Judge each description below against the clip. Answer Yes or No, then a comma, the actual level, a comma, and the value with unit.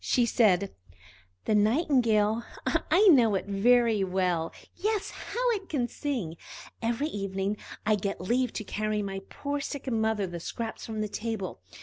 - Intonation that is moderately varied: Yes, average, 4.3 semitones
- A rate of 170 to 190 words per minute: No, average, 145 wpm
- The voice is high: Yes, high, 220 Hz